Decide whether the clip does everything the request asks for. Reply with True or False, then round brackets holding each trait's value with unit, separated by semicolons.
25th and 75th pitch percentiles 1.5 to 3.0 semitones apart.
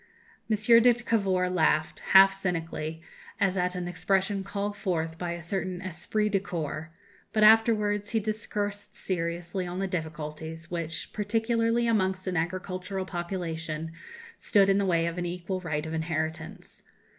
False (3.4 semitones)